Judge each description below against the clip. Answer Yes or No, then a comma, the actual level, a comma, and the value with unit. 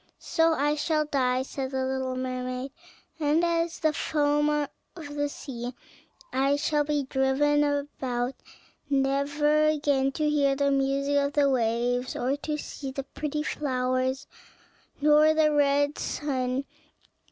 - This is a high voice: Yes, very high, 285 Hz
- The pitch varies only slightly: Yes, narrow, 2.1 semitones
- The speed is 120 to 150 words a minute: Yes, slow, 135 wpm